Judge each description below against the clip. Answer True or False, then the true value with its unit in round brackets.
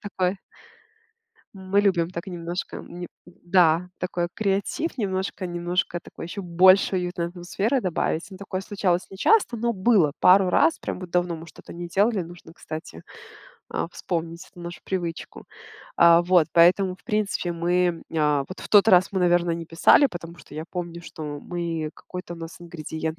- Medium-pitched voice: True (175 Hz)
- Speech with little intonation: True (2.1 semitones)